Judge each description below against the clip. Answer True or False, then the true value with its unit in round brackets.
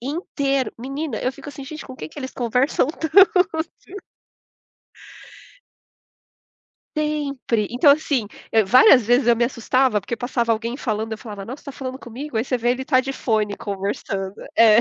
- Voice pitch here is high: True (255 Hz)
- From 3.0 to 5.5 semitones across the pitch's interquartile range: True (3.9 semitones)